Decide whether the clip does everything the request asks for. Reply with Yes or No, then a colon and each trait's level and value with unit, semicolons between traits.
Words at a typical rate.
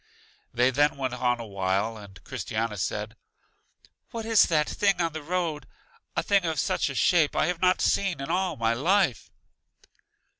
Yes: average, 175 wpm